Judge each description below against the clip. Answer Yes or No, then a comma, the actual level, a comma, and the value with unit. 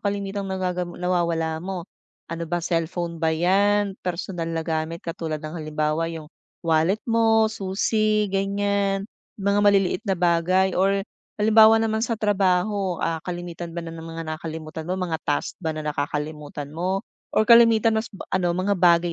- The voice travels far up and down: No, average, 3.4 semitones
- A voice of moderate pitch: Yes, medium, 180 Hz